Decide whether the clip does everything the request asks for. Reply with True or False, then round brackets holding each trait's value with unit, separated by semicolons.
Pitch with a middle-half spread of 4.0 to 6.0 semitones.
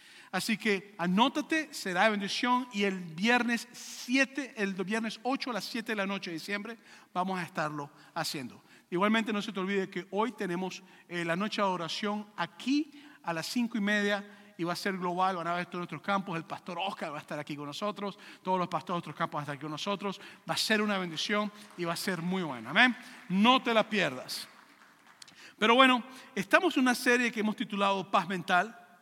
True (4.6 semitones)